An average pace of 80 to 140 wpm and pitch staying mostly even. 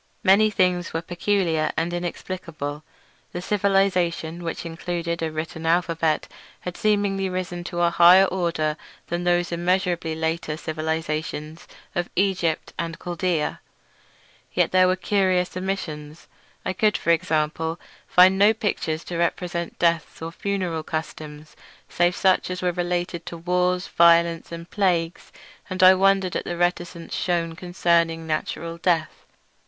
Yes: slow, 135 wpm; narrow, 1.9 semitones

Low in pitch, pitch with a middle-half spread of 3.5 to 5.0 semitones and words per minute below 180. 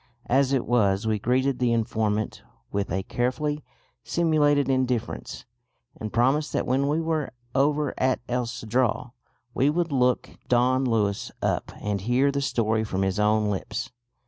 Yes: low, 125 Hz; average, 4.2 semitones; average, 150 wpm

